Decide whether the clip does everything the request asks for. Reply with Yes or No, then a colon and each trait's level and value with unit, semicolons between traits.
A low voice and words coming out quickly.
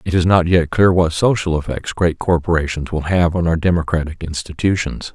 No: very low, 85 Hz; average, 185 wpm